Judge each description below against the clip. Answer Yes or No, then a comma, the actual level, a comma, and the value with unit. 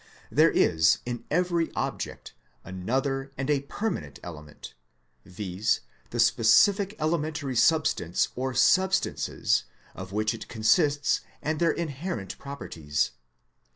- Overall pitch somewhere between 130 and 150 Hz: Yes, low, 135 Hz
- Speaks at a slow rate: Yes, slow, 115 wpm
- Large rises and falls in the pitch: Yes, wide, 8.0 semitones